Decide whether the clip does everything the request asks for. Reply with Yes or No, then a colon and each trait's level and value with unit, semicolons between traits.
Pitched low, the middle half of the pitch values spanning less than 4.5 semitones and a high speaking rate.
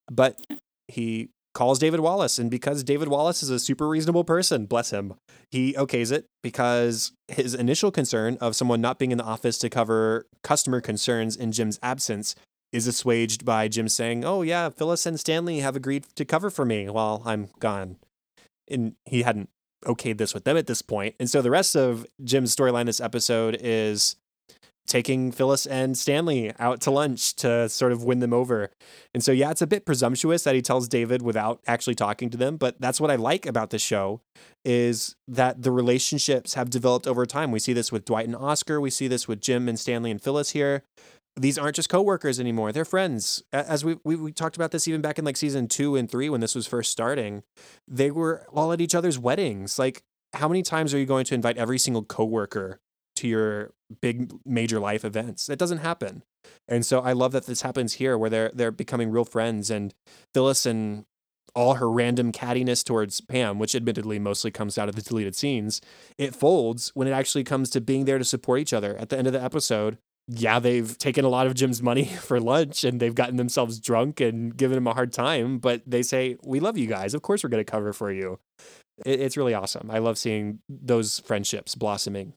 Yes: low, 125 Hz; average, 3.2 semitones; fast, 210 wpm